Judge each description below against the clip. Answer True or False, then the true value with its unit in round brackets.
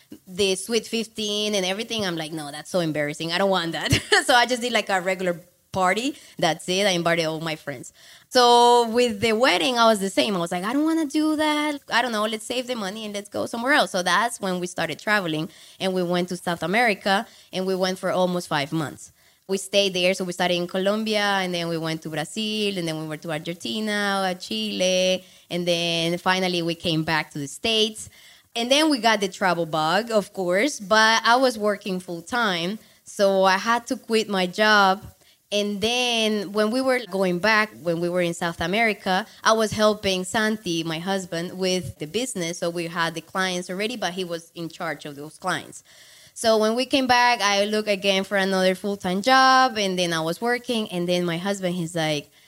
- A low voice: False (195 Hz)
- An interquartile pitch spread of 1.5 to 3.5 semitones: False (3.9 semitones)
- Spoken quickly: True (220 wpm)